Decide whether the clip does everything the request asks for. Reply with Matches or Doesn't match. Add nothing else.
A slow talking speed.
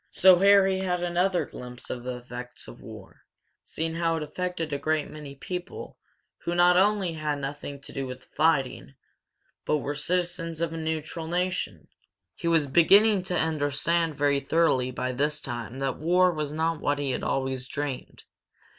Doesn't match